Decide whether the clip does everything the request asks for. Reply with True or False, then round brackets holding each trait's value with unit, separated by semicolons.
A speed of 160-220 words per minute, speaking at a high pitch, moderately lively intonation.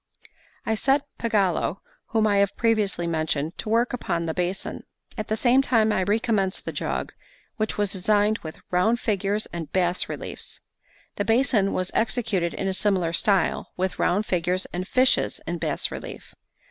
True (165 wpm; 200 Hz; 3.5 semitones)